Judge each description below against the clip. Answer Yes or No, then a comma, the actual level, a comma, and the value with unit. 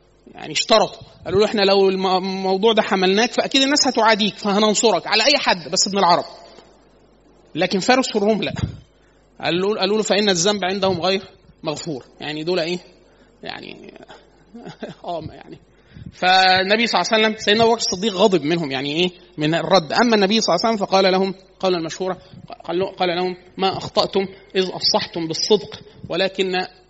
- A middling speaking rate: No, fast, 155 wpm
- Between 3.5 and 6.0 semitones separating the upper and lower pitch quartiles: No, average, 2.9 semitones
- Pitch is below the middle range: No, high, 190 Hz